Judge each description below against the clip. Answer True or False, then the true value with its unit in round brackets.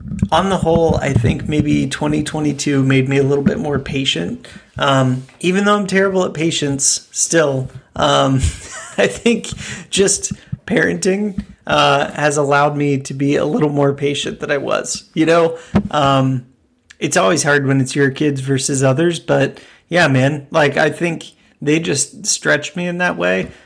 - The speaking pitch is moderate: True (145 Hz)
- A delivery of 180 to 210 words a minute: False (165 wpm)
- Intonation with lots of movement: False (3.8 semitones)